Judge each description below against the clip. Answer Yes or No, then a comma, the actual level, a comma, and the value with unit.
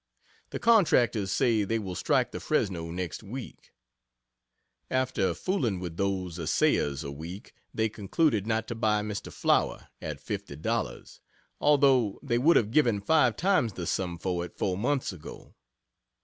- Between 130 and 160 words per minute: Yes, average, 150 wpm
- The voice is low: Yes, low, 105 Hz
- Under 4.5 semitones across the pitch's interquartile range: No, average, 5.3 semitones